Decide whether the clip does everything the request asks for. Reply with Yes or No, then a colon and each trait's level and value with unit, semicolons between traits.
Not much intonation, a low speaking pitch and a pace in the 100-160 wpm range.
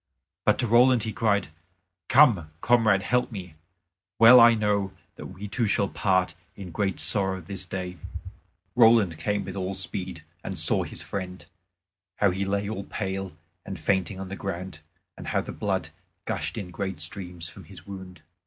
No: narrow, 2.2 semitones; very low, 95 Hz; average, 170 wpm